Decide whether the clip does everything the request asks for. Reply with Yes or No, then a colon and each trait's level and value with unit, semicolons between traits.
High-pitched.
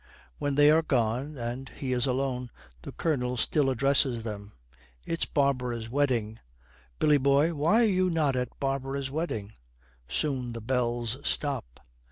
No: low, 135 Hz